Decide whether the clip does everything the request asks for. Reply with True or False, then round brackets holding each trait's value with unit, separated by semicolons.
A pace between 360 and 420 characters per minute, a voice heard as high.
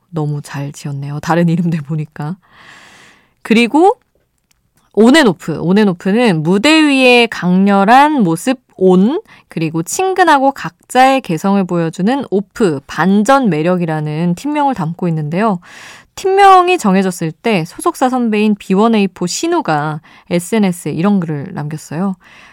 False (275 characters per minute; 195 Hz)